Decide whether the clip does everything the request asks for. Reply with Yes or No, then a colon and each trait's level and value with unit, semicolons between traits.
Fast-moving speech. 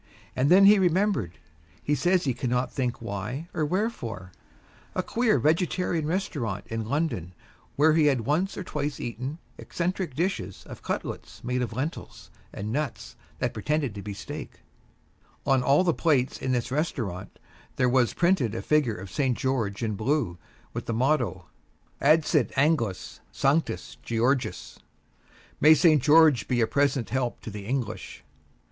No: average, 155 wpm